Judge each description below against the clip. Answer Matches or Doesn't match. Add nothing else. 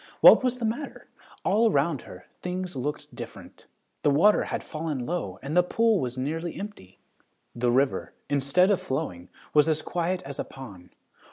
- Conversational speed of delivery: Matches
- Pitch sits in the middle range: Matches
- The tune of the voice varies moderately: Doesn't match